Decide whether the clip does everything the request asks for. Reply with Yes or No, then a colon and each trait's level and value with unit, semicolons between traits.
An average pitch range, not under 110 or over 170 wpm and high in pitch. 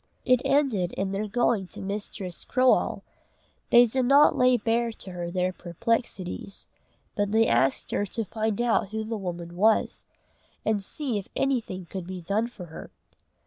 Yes: average, 4.3 semitones; average, 165 wpm; high, 210 Hz